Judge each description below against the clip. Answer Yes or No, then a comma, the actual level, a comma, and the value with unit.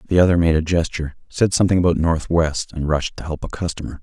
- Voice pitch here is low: Yes, very low, 85 Hz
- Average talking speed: No, fast, 225 wpm